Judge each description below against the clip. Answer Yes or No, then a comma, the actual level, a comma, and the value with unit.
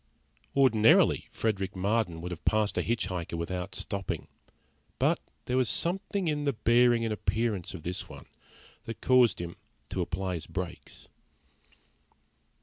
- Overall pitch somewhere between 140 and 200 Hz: No, low, 105 Hz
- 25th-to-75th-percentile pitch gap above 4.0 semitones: Yes, average, 4.7 semitones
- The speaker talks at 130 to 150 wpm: Yes, average, 145 wpm